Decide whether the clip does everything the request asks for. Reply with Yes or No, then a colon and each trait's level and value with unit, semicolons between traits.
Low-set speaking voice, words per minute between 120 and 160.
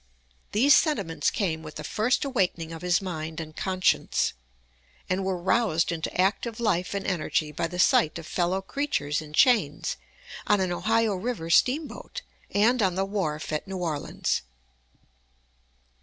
No: medium, 185 Hz; average, 150 wpm